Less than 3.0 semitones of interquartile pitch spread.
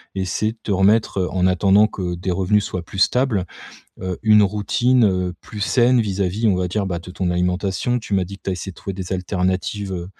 Yes: narrow, 2.4 semitones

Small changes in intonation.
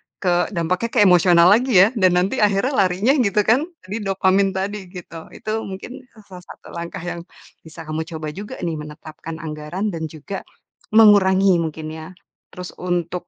No: average, 3.3 semitones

